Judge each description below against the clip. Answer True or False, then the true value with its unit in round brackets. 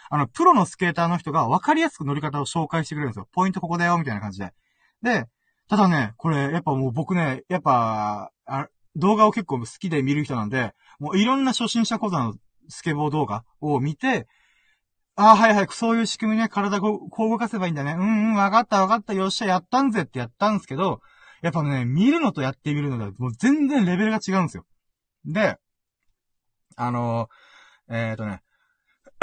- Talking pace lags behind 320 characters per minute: False (395 characters per minute)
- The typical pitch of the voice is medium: True (175 Hz)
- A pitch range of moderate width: False (8.0 semitones)